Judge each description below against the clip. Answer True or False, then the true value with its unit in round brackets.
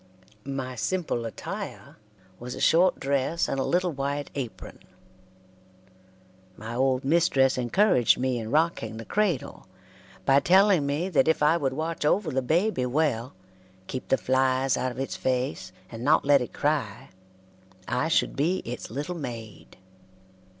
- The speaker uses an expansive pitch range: False (4.3 semitones)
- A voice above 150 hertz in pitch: False (135 Hz)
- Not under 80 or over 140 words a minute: False (150 wpm)